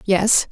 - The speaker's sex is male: No, female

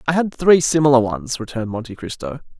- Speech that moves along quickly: No, average, 185 wpm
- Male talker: Yes, male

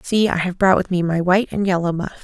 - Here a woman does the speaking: Yes, female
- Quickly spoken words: Yes, fast, 295 wpm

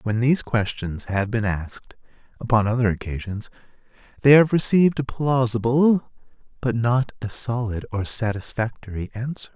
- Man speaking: Yes, male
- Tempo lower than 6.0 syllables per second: Yes, 5.0 syllables/s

